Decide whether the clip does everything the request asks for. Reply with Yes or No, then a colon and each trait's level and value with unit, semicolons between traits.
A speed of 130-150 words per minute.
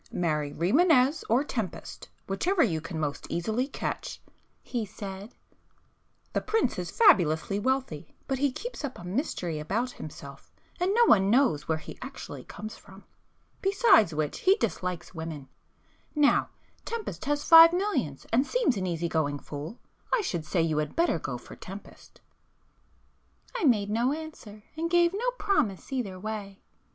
Yes: average, 145 wpm